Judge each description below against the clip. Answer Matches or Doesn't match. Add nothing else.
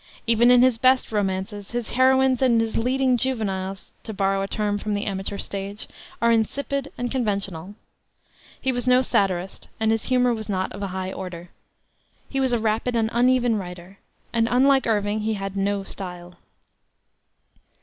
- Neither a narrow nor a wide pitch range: Matches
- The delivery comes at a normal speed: Matches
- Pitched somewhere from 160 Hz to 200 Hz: Doesn't match